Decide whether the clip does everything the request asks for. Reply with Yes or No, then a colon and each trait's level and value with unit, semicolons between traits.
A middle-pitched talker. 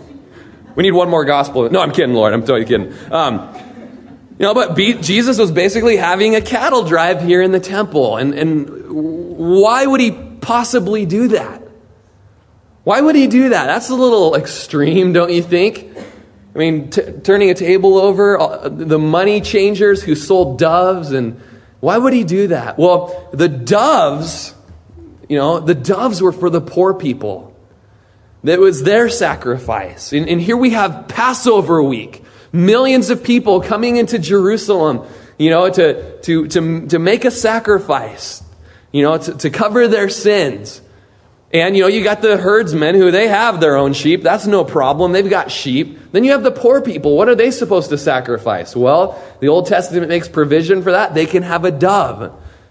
Yes: medium, 180 Hz